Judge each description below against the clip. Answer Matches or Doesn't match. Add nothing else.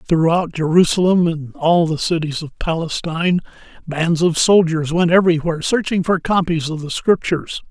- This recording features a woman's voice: Doesn't match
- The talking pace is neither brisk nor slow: Matches